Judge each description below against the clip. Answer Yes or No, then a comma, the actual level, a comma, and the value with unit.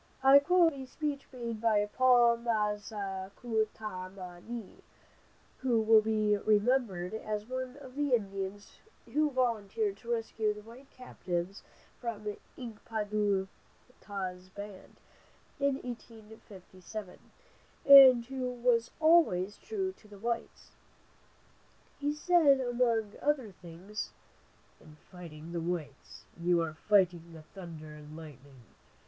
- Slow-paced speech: Yes, slow, 130 wpm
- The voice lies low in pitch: No, high, 215 Hz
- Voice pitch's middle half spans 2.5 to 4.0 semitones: No, average, 4.9 semitones